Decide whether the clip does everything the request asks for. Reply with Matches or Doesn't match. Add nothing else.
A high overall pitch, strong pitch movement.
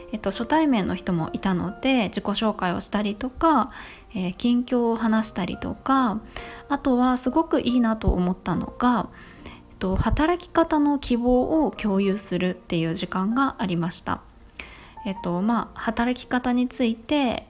Doesn't match